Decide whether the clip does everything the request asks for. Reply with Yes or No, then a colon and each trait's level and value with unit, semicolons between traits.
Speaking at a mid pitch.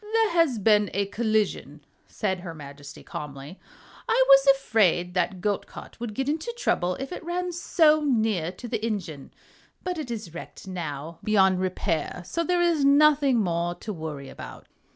No: high, 210 Hz